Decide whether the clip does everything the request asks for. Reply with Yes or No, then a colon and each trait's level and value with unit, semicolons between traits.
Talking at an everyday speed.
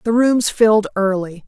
Yes: average, 165 wpm